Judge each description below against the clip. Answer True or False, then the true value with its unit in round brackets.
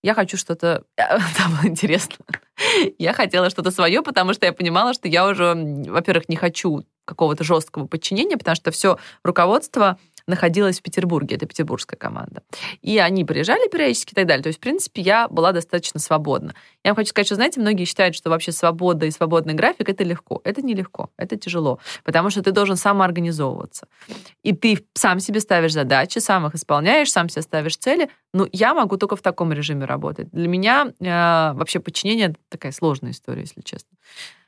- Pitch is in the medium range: True (180 Hz)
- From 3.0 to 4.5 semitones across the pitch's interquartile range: True (3.6 semitones)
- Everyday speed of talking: False (180 wpm)